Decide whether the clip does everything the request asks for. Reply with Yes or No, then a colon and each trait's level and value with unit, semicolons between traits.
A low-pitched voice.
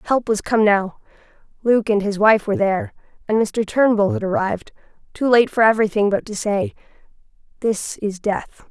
No: high, 215 Hz